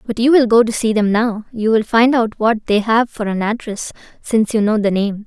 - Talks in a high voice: Yes, high, 220 Hz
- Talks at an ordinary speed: No, fast, 240 wpm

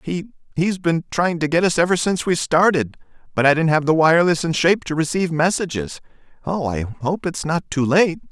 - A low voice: No, medium, 160 Hz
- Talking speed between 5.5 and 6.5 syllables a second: Yes, 5.6 syllables/s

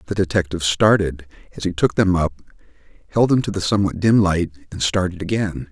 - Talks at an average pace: Yes, average, 190 wpm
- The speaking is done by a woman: No, male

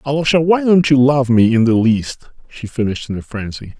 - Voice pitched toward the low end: Yes, low, 130 Hz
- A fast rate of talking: Yes, fast, 220 wpm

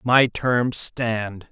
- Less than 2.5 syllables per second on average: Yes, 2.1 syllables/s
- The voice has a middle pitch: No, low, 115 Hz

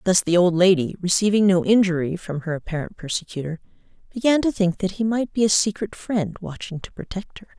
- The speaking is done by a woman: Yes, female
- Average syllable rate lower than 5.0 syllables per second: No, 5.7 syllables/s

